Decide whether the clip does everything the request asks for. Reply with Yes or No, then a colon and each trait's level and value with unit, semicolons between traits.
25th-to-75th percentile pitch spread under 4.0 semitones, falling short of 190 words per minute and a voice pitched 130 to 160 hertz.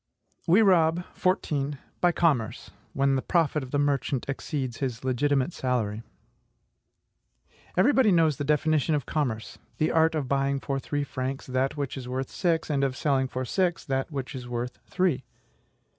Yes: average, 3.6 semitones; average, 160 wpm; medium, 140 Hz